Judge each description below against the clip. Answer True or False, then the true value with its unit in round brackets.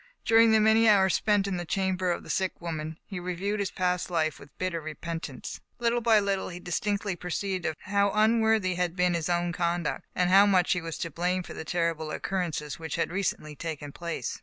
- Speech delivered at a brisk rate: True (210 wpm)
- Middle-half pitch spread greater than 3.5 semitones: False (3.0 semitones)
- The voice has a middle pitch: True (180 Hz)